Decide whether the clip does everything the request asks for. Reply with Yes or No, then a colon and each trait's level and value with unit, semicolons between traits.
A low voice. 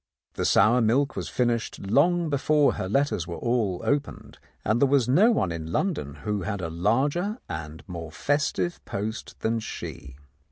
Yes: low, 115 Hz